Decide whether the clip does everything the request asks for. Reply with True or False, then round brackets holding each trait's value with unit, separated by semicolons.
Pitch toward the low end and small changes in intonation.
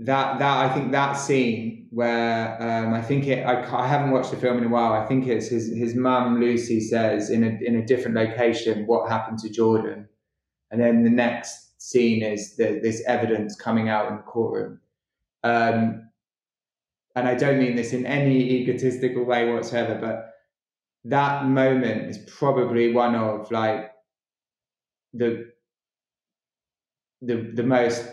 True (120 Hz; 2.0 semitones)